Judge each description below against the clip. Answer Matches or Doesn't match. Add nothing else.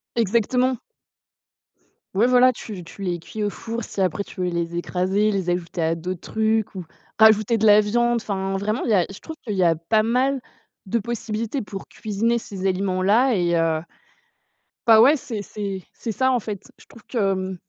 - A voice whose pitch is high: Matches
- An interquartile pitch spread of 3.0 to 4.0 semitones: Matches